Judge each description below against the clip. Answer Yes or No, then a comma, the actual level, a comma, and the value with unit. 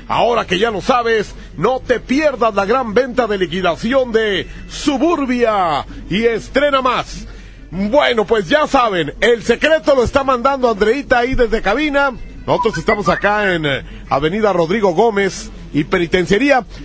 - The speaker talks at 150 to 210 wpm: No, average, 140 wpm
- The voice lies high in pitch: Yes, high, 230 Hz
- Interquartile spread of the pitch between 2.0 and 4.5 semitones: No, average, 5.1 semitones